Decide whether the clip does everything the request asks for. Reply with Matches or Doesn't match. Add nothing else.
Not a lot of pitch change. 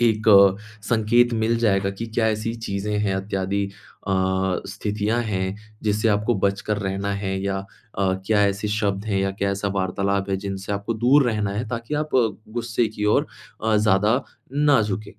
Matches